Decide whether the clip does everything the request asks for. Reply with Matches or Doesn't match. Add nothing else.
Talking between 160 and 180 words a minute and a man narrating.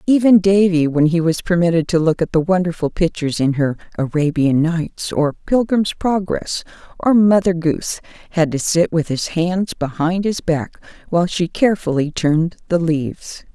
Doesn't match